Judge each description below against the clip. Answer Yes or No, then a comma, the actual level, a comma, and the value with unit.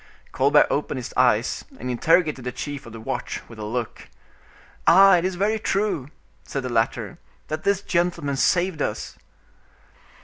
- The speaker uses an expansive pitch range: Yes, wide, 6.4 semitones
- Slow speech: No, average, 150 wpm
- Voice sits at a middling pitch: Yes, medium, 145 Hz